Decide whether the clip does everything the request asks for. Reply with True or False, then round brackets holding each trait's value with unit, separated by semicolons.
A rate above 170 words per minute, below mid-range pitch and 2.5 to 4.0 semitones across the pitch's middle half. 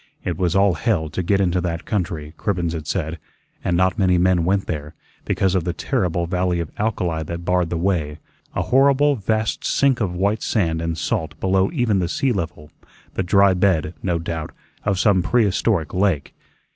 True (185 wpm; 90 Hz; 3.1 semitones)